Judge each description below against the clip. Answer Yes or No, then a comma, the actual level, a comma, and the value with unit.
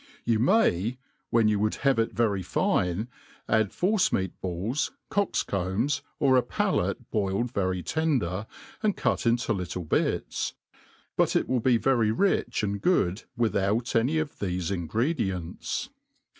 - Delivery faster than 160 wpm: No, average, 145 wpm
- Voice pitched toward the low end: Yes, low, 110 Hz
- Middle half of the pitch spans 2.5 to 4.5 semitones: No, wide, 5.4 semitones